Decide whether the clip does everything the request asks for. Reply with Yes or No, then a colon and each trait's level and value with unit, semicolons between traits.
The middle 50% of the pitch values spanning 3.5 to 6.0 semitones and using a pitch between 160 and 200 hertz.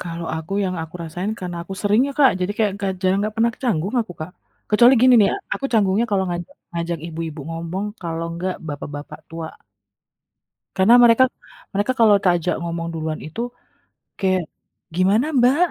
Yes: average, 4.2 semitones; medium, 185 Hz